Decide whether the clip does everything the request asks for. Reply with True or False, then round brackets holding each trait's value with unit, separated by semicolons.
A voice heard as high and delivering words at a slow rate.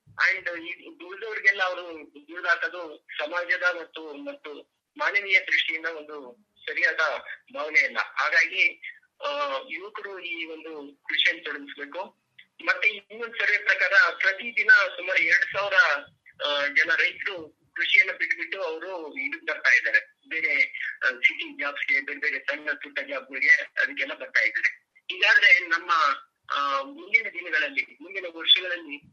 True (205 Hz; 110 wpm)